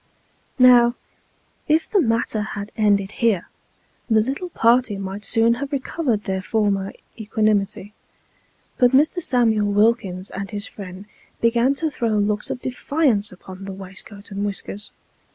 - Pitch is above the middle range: Yes, high, 215 Hz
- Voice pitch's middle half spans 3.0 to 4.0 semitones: Yes, average, 3.5 semitones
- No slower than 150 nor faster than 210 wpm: No, slow, 135 wpm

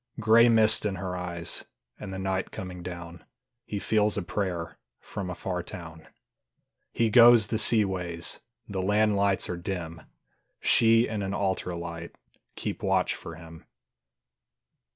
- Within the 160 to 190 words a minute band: No, average, 150 wpm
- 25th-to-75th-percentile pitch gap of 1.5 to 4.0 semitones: Yes, average, 3.5 semitones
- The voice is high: No, very low, 95 Hz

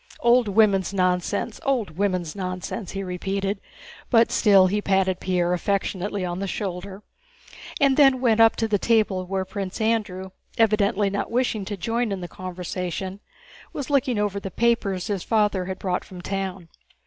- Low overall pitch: No, high, 195 Hz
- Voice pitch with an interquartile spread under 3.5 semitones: Yes, average, 2.9 semitones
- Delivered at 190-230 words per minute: No, average, 160 wpm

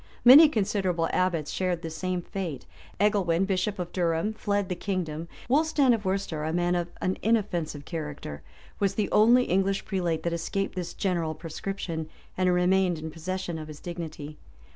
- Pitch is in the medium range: Yes, medium, 180 Hz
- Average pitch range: Yes, average, 3.1 semitones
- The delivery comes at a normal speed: Yes, average, 165 wpm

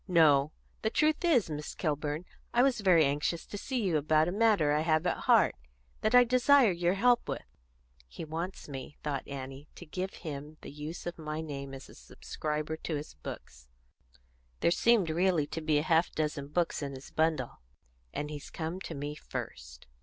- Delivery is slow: No, average, 190 wpm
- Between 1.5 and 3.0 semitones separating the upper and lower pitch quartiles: No, average, 3.8 semitones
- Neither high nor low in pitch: Yes, medium, 160 Hz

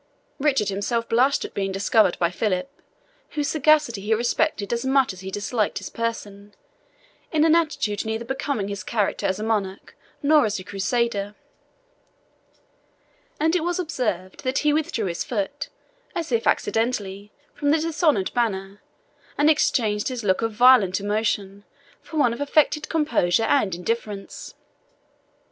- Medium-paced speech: Yes, average, 150 wpm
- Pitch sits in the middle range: No, high, 225 Hz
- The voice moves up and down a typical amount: No, wide, 6.0 semitones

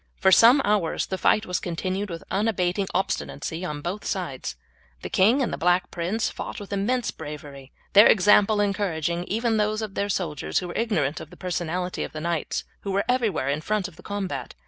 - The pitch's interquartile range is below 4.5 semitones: Yes, average, 3.5 semitones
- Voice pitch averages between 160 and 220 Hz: Yes, high, 190 Hz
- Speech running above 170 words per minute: Yes, average, 195 wpm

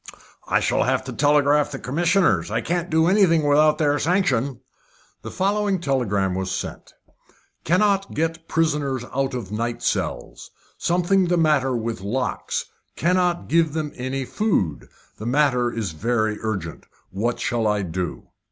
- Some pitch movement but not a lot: No, wide, 6.4 semitones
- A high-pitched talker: No, medium, 145 Hz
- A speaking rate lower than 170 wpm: Yes, average, 150 wpm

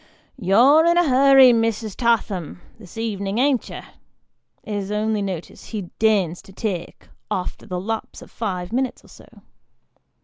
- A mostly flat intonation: No, average, 3.9 semitones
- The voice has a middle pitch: No, high, 215 Hz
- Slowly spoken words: No, average, 165 wpm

